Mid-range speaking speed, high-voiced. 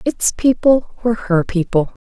Yes: average, 145 wpm; high, 215 Hz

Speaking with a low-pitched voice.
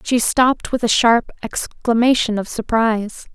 No: high, 230 Hz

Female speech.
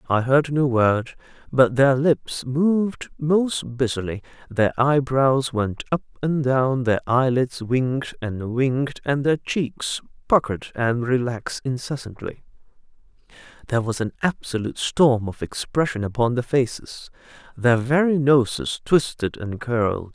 No: male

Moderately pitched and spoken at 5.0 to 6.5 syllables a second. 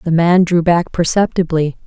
No: medium, 170 Hz; 4.7 syllables/s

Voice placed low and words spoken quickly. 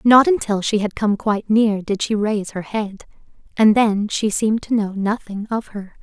No: high, 210 Hz; fast, 210 wpm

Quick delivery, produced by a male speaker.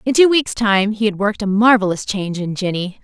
No: fast, 235 wpm; female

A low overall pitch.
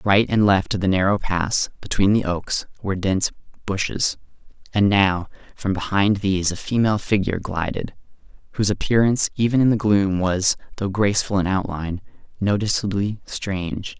Yes: low, 100 Hz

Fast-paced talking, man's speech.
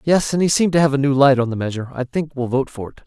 Yes: fast, 350 wpm; male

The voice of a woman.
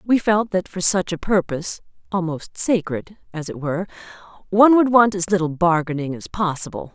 Yes: female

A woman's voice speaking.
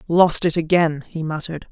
Yes: female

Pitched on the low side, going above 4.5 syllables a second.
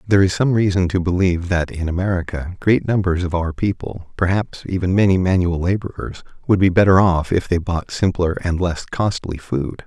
Yes: very low, 90 Hz; 5.2 syllables/s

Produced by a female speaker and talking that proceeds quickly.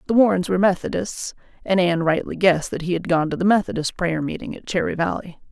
Yes: female; fast, 220 wpm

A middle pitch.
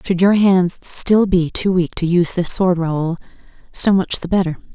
Yes: medium, 180 Hz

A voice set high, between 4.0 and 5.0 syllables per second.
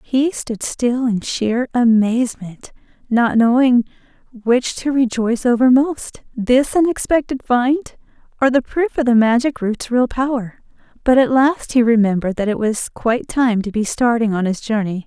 Yes: high, 240 Hz; 4.5 syllables/s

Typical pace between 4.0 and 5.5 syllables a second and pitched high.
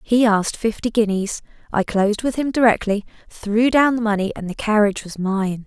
Yes: 5.4 syllables/s; high, 215 Hz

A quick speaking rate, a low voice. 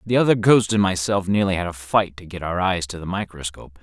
Yes: fast, 250 wpm; very low, 95 Hz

